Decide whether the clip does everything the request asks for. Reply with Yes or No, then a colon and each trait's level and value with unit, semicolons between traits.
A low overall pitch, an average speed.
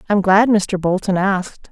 No: high, 195 Hz; average, 175 wpm